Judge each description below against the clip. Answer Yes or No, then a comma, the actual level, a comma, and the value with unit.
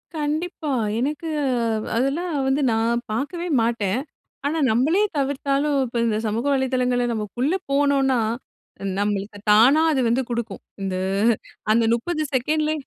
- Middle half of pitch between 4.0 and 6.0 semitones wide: Yes, average, 4.3 semitones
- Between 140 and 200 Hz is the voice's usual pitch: No, very high, 265 Hz